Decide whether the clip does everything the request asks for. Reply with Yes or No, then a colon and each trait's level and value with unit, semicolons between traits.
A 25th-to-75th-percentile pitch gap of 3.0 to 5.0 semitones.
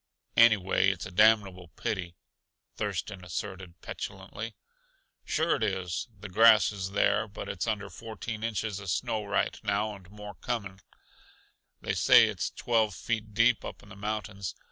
No: narrow, 2.6 semitones